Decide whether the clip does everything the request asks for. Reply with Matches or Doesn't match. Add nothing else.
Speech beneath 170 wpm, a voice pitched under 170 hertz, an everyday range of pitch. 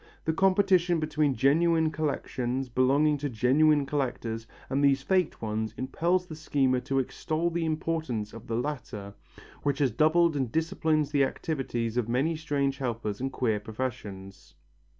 Matches